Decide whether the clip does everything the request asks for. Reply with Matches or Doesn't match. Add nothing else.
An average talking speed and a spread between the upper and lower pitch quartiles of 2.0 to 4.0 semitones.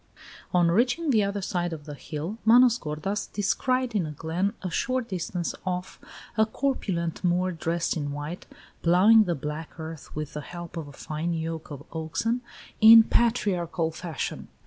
Doesn't match